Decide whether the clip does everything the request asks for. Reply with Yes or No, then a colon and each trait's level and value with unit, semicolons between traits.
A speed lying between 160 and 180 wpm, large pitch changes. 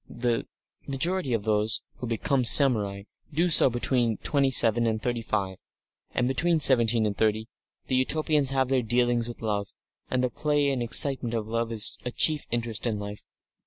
No: average, 175 wpm; average, 3.3 semitones